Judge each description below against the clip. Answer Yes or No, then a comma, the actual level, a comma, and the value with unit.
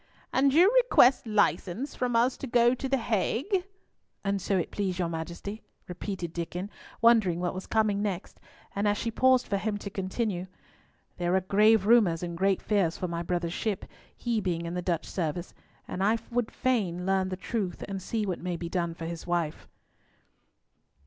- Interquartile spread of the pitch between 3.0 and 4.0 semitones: No, average, 4.4 semitones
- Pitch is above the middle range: Yes, high, 195 Hz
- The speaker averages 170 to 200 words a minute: Yes, average, 175 wpm